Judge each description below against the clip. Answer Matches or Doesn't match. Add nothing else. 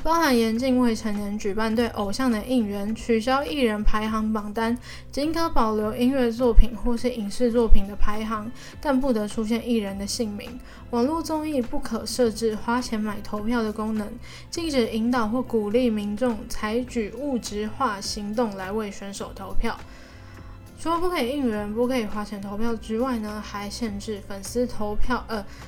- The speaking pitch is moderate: Doesn't match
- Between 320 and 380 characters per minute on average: Doesn't match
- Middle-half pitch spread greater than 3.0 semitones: Doesn't match